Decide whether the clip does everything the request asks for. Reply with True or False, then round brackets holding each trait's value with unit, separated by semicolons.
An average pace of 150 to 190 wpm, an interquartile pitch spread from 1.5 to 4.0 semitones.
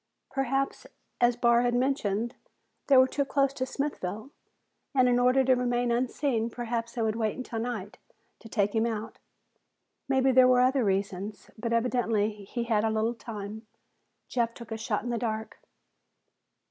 True (165 wpm; 2.5 semitones)